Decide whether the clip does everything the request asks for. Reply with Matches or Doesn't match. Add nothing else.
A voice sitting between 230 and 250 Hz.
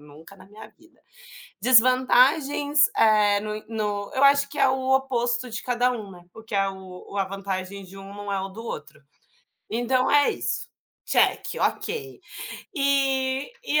Matches